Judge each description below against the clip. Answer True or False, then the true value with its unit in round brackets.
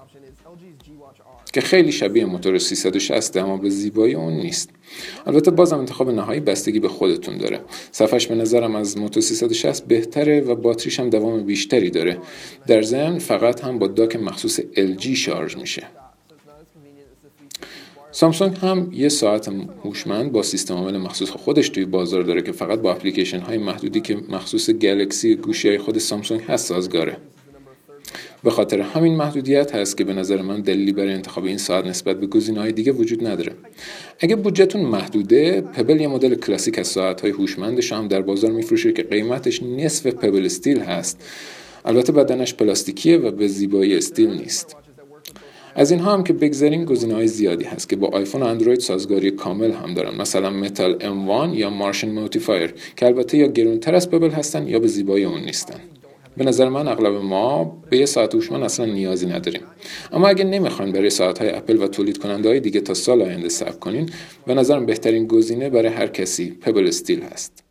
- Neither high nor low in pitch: False (130 Hz)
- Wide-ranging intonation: True (8.9 semitones)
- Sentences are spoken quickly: True (170 wpm)